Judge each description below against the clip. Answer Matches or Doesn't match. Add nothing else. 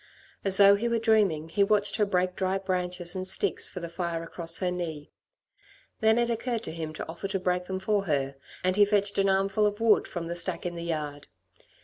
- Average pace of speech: Doesn't match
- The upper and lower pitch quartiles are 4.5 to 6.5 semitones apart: Doesn't match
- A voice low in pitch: Doesn't match